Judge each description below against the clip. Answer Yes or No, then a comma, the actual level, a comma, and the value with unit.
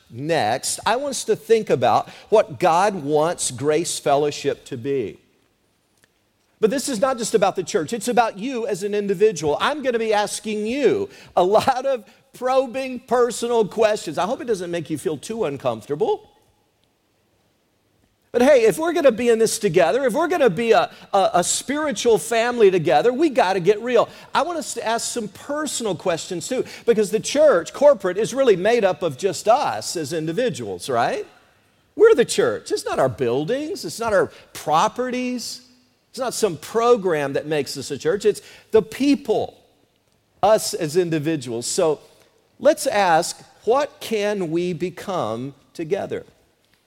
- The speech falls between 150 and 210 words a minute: Yes, average, 170 wpm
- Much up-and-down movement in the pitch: Yes, wide, 6.9 semitones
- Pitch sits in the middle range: No, high, 225 Hz